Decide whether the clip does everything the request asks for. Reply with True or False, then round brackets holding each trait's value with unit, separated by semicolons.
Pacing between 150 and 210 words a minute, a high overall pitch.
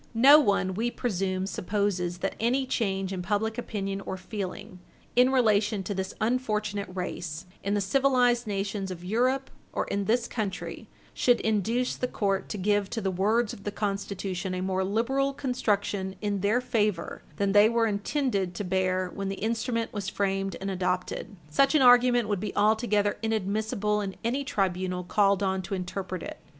True (170 wpm; 205 Hz)